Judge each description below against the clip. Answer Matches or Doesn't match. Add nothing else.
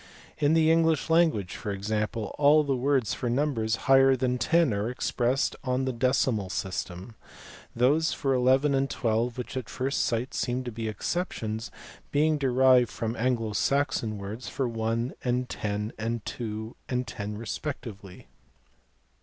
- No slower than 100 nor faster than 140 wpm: Doesn't match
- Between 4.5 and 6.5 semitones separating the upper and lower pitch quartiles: Doesn't match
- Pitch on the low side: Matches